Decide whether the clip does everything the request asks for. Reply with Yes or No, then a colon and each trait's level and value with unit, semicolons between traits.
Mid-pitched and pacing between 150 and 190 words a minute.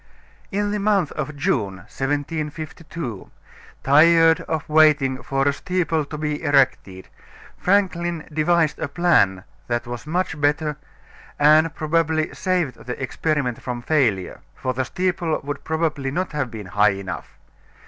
No: medium, 150 Hz; slow, 135 wpm